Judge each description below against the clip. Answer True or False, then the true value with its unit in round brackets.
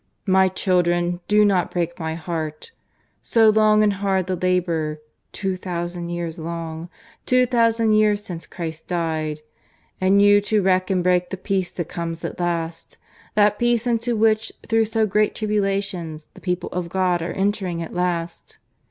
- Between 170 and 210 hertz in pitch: True (185 Hz)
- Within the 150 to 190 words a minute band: True (160 wpm)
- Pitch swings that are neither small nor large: True (3.5 semitones)